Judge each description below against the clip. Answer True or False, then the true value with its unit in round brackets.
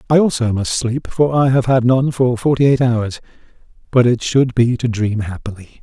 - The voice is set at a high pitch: False (120 Hz)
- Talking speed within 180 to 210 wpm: True (195 wpm)